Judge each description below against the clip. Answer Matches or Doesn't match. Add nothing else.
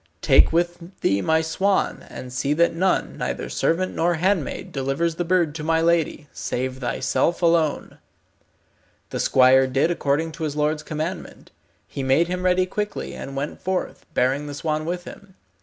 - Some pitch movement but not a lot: Matches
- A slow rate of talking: Doesn't match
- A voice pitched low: Doesn't match